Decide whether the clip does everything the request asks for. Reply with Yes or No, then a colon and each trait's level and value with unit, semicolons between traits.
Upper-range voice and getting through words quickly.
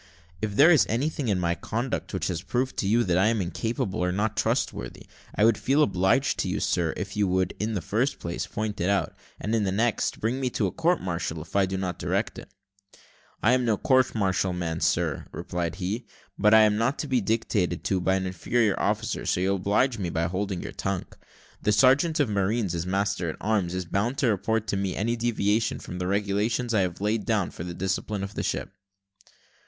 No: low, 100 Hz; fast, 220 wpm